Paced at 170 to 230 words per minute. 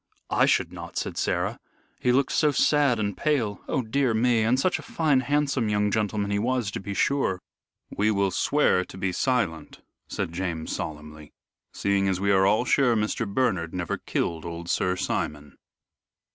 Yes: average, 175 wpm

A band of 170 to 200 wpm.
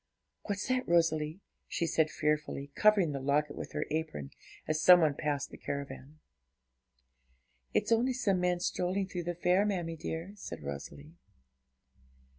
No: average, 145 wpm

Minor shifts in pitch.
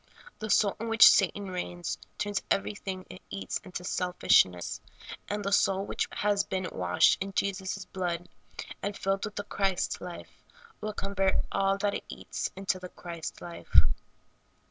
Yes: narrow, 2.0 semitones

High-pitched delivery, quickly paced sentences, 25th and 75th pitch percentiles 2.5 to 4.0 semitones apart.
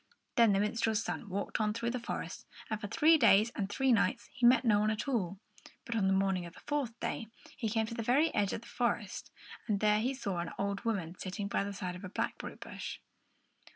Yes: high, 215 Hz; fast, 235 wpm; average, 3.0 semitones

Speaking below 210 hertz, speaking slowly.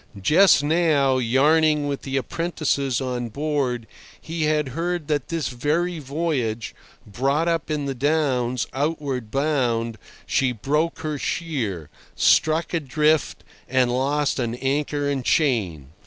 Yes: medium, 140 Hz; slow, 125 wpm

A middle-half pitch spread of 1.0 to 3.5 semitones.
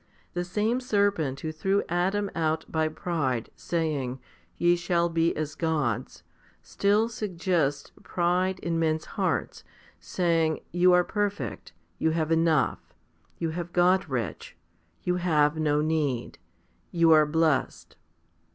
Yes: narrow, 2.5 semitones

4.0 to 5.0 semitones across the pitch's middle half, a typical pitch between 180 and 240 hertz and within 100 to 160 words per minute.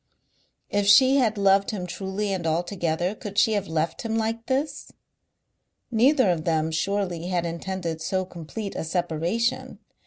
Yes: average, 4.4 semitones; high, 190 Hz; average, 150 wpm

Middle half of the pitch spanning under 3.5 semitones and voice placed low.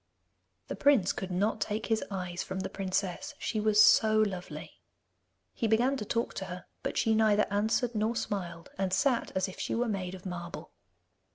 No: average, 3.0 semitones; high, 205 Hz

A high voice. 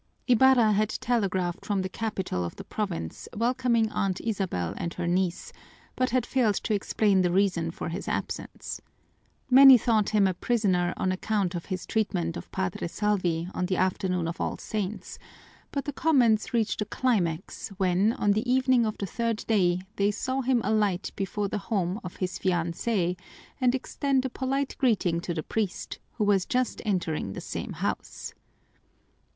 Yes: high, 205 Hz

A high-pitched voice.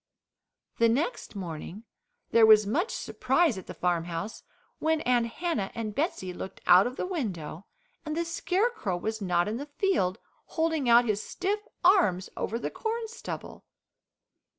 Yes: high, 235 Hz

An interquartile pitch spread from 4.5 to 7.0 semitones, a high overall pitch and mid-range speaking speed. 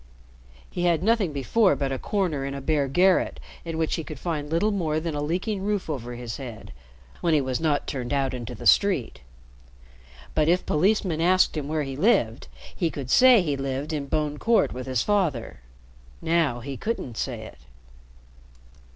No: average, 4.8 semitones; medium, 155 Hz; average, 185 wpm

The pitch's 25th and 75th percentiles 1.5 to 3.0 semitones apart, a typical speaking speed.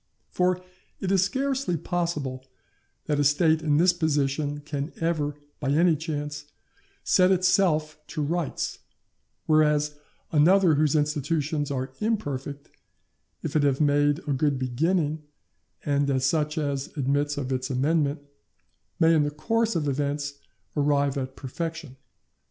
No: narrow, 2.5 semitones; slow, 130 wpm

